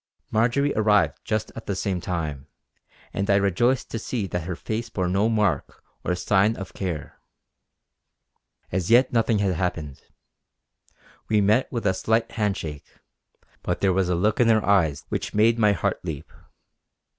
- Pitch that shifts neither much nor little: Yes, average, 3.8 semitones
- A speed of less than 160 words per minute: No, average, 165 wpm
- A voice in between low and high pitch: No, low, 100 Hz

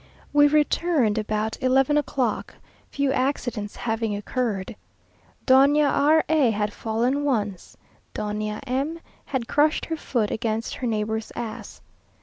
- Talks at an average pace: No, slow, 125 wpm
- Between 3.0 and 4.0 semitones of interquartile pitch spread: No, average, 4.7 semitones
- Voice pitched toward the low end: No, high, 245 Hz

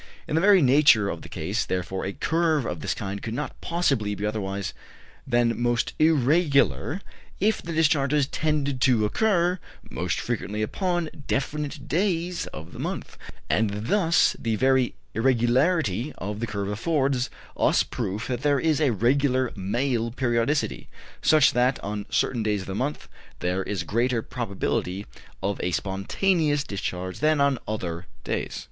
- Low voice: Yes, low, 125 Hz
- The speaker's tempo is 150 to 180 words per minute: Yes, average, 155 wpm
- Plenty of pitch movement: Yes, wide, 6.4 semitones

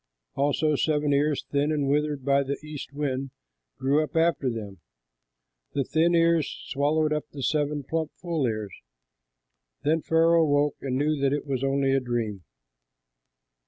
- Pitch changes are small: Yes, narrow, 2.2 semitones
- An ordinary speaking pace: Yes, average, 155 wpm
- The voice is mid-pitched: Yes, medium, 145 Hz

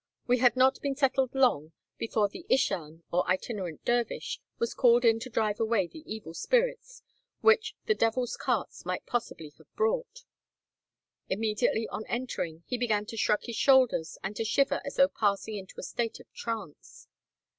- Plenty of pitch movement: No, average, 4.3 semitones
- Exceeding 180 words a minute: No, average, 165 wpm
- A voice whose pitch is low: No, high, 230 Hz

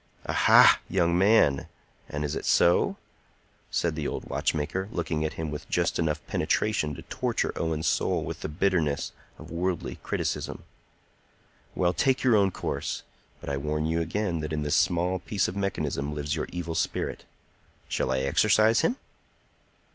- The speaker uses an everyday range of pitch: Yes, average, 3.8 semitones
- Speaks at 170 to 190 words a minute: No, average, 160 wpm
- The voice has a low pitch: Yes, very low, 85 Hz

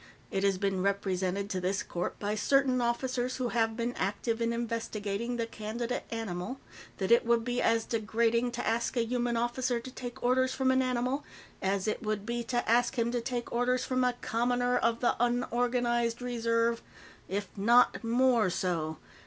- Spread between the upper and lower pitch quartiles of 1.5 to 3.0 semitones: Yes, narrow, 2.4 semitones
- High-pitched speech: Yes, high, 235 Hz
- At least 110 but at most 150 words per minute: No, average, 180 wpm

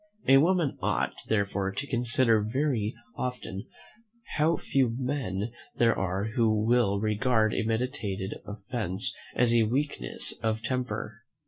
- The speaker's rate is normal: No, slow, 125 wpm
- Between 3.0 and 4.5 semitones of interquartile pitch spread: Yes, average, 3.4 semitones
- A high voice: No, low, 115 Hz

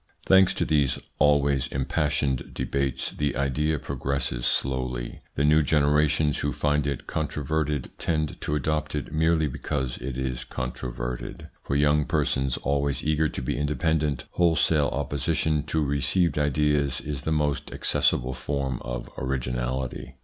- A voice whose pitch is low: Yes, very low, 70 Hz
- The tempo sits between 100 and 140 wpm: Yes, slow, 135 wpm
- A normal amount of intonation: No, narrow, 2.3 semitones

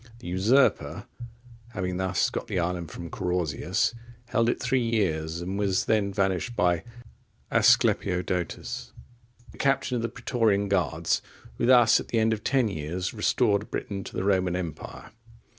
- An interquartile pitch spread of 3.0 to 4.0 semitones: No, average, 4.4 semitones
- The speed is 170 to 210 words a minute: No, average, 155 wpm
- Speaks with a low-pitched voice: Yes, low, 100 Hz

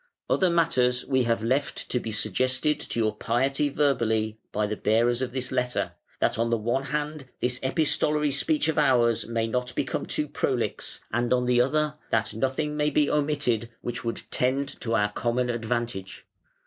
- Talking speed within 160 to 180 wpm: Yes, average, 175 wpm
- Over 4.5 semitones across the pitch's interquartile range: No, average, 3.6 semitones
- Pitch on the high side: No, low, 125 Hz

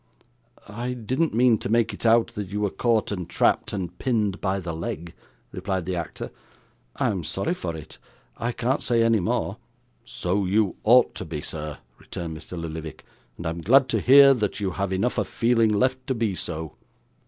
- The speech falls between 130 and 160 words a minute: No, average, 190 wpm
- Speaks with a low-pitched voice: Yes, low, 100 Hz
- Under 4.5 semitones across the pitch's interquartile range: No, average, 5.1 semitones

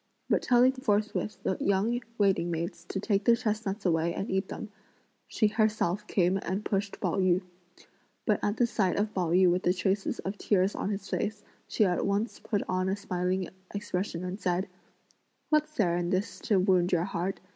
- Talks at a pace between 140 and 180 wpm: No, average, 190 wpm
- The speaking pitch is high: Yes, high, 195 Hz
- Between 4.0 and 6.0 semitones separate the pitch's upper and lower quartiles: No, narrow, 2.6 semitones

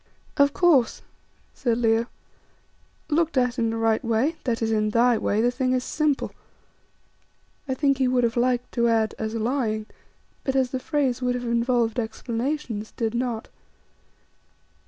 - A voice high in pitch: Yes, high, 245 Hz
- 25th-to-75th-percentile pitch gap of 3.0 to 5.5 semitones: No, narrow, 2.5 semitones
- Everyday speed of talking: Yes, average, 155 wpm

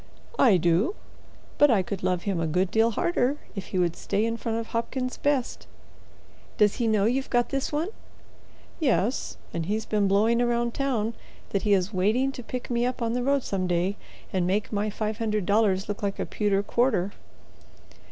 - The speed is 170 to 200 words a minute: Yes, average, 190 wpm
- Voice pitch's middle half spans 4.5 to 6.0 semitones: No, average, 3.7 semitones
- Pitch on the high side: Yes, high, 215 Hz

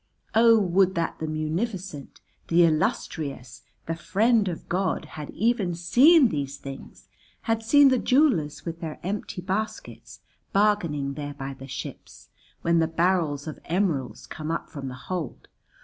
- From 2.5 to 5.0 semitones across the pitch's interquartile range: No, wide, 5.6 semitones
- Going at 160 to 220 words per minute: No, average, 150 wpm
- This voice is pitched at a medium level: Yes, medium, 170 Hz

